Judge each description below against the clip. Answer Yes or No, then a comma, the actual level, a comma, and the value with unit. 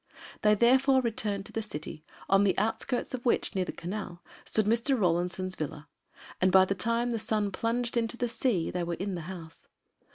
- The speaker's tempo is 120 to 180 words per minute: No, average, 195 wpm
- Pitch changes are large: No, average, 4.3 semitones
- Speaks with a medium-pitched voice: No, high, 205 Hz